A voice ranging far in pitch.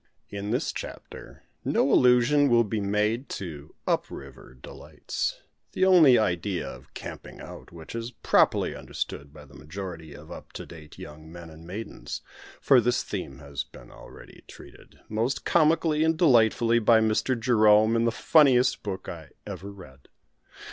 Yes: wide, 7.0 semitones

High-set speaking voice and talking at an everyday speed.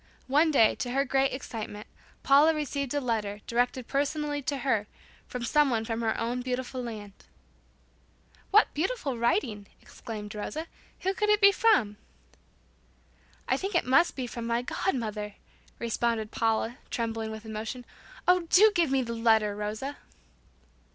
Yes: high, 245 Hz; average, 150 wpm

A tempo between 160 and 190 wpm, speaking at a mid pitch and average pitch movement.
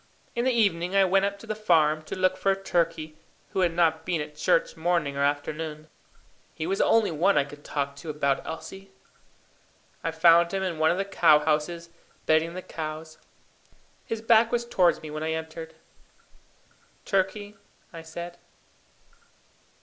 Yes: average, 170 wpm; medium, 165 Hz; average, 3.6 semitones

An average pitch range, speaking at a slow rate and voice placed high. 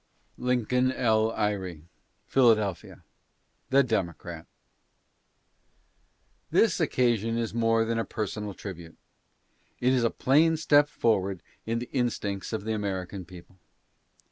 No: average, 4.0 semitones; slow, 115 wpm; low, 110 Hz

